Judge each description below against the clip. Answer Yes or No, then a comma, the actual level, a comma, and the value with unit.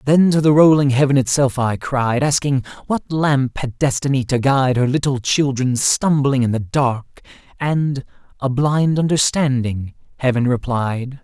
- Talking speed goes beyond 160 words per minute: No, average, 145 wpm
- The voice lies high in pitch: No, low, 135 Hz